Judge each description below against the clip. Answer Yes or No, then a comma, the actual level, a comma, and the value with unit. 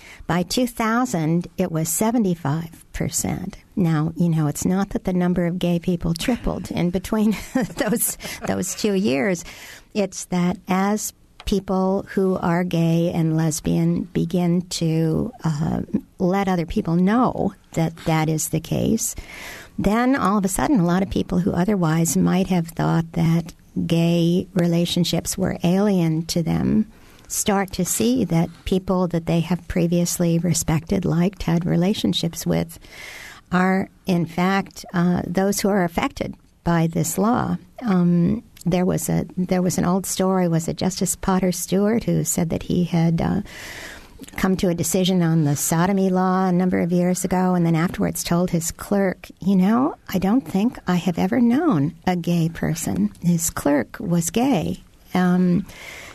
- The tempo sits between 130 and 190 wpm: Yes, average, 155 wpm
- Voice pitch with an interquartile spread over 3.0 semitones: No, narrow, 2.5 semitones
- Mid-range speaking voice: Yes, medium, 180 Hz